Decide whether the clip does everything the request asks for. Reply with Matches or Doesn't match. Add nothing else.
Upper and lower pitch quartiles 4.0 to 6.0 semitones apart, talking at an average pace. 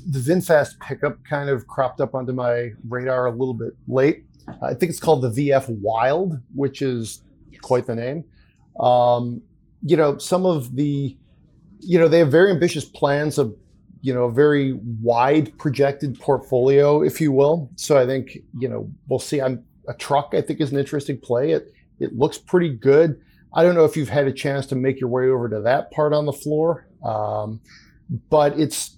Doesn't match